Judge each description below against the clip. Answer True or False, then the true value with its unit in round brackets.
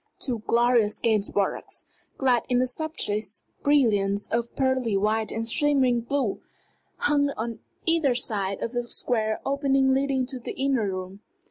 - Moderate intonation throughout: True (3.8 semitones)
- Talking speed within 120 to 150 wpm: True (140 wpm)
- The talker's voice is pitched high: True (240 Hz)